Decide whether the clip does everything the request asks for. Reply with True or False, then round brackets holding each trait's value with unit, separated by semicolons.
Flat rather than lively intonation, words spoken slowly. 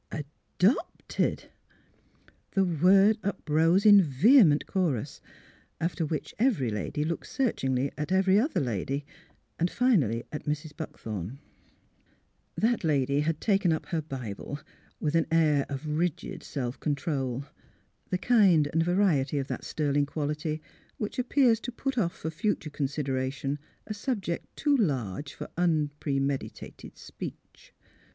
False (5.4 semitones; 130 wpm)